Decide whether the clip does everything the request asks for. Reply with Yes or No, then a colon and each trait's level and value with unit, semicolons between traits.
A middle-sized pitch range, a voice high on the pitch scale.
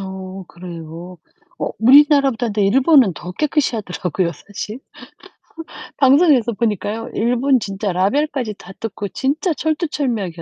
No: wide, 6.3 semitones; high, 220 Hz